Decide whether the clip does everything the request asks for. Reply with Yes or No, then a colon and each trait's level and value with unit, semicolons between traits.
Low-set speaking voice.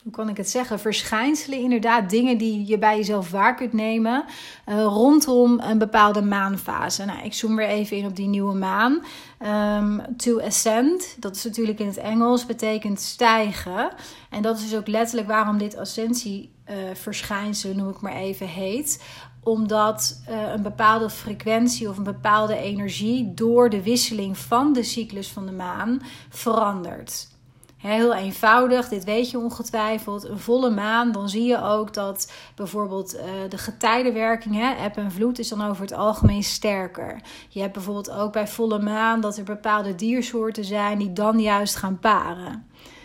No: high, 215 Hz